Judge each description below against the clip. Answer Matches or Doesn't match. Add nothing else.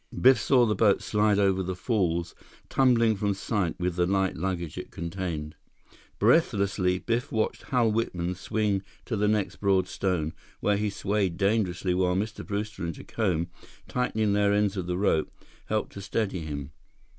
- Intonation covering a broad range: Doesn't match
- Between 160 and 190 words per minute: Matches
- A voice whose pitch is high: Doesn't match